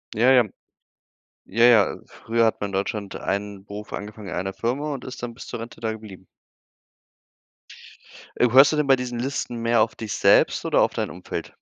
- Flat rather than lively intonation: No, average, 3.0 semitones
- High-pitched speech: No, low, 115 Hz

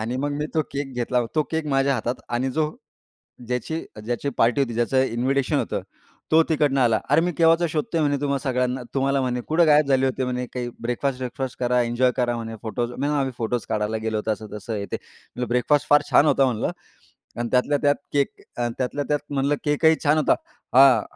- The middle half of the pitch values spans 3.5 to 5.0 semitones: No, average, 3.1 semitones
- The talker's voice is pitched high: No, low, 130 Hz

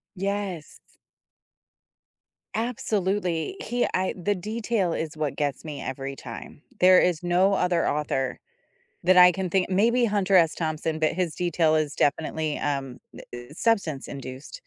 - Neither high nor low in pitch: Yes, medium, 175 Hz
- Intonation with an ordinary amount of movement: Yes, average, 4.4 semitones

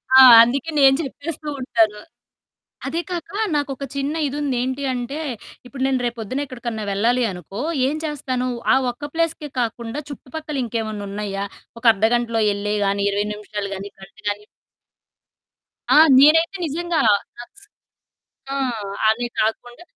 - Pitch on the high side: Yes, very high, 250 Hz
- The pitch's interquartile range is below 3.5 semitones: No, average, 4.8 semitones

